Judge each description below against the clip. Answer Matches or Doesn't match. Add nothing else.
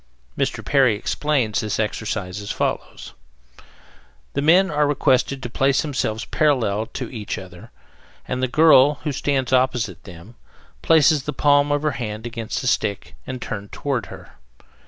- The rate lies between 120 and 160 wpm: Matches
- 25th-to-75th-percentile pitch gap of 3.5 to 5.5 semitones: Matches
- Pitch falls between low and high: Doesn't match